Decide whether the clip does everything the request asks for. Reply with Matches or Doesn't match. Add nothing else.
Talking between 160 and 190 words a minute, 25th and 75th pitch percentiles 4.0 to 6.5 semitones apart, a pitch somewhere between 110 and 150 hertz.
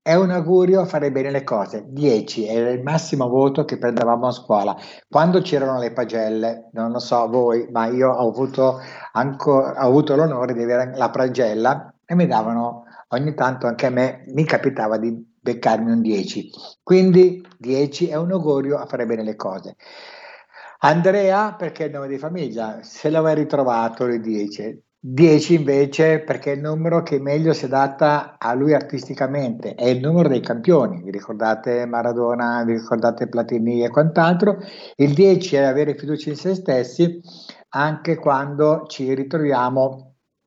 Matches